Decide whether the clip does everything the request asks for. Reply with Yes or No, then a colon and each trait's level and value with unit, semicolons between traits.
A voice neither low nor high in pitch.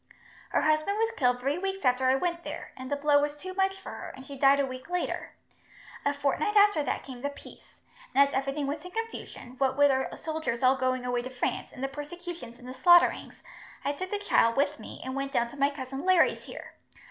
No: very high, 280 Hz